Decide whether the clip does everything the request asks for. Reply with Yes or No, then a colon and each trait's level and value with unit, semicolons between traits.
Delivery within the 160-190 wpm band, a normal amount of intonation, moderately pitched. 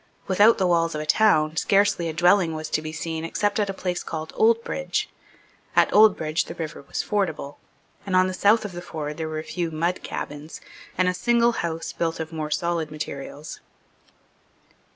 Yes: average, 185 wpm; average, 3.8 semitones; medium, 170 Hz